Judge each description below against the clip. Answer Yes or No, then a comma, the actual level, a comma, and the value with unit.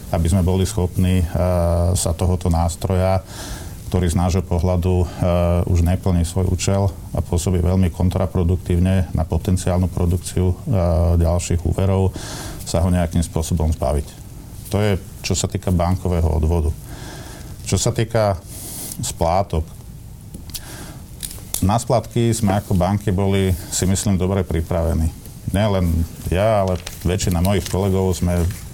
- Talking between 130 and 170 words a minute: No, average, 120 wpm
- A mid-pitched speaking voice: No, very low, 90 Hz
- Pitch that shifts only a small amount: Yes, narrow, 2.0 semitones